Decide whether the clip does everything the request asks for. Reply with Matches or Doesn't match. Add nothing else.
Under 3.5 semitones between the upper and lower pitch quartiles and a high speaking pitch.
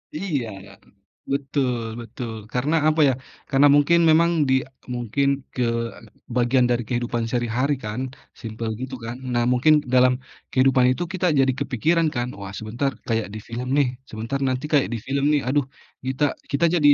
Doesn't match